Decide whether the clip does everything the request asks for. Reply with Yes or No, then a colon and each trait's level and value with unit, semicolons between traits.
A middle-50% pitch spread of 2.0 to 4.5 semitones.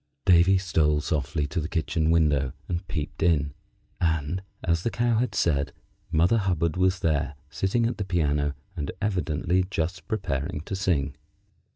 Yes: average, 3.9 semitones